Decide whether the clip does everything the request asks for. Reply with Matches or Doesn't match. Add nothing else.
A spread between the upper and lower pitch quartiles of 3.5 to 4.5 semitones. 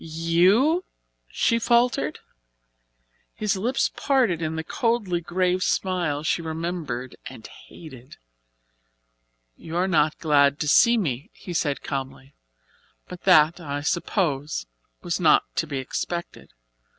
Matches